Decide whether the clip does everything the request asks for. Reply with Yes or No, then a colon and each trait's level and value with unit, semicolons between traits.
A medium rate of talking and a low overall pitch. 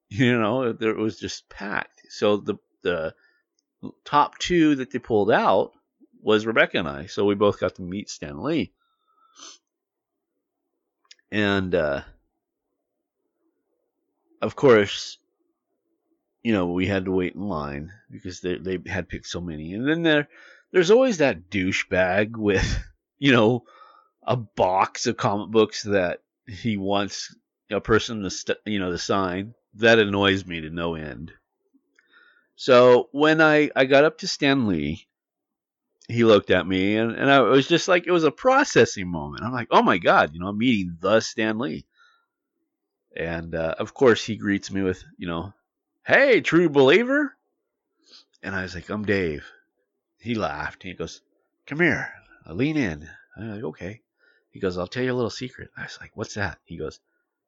Yes: average, 170 wpm; low, 115 Hz